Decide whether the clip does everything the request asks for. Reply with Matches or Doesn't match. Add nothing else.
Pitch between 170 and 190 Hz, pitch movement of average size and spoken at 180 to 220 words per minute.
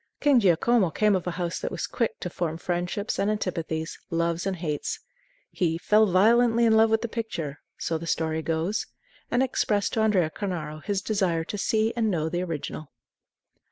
Matches